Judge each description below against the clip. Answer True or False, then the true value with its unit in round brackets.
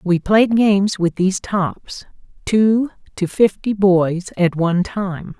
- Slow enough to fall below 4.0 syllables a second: True (3.6 syllables/s)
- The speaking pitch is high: True (195 Hz)